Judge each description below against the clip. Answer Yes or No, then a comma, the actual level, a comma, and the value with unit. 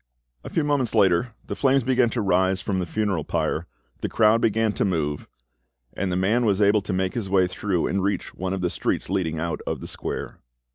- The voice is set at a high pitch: No, low, 100 Hz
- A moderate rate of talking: No, fast, 220 wpm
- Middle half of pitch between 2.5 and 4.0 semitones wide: Yes, average, 3.4 semitones